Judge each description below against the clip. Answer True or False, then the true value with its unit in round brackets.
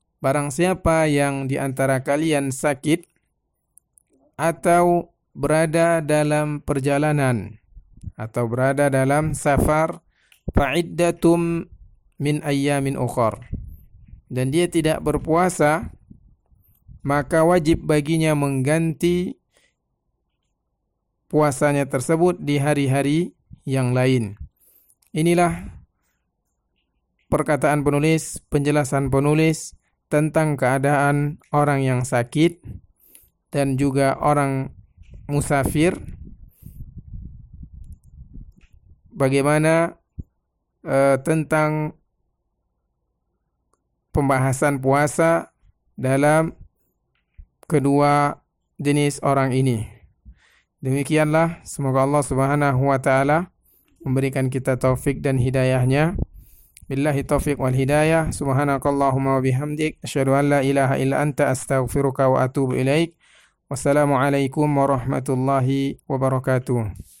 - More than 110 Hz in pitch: True (140 Hz)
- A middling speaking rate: False (80 wpm)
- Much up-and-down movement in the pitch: False (2.6 semitones)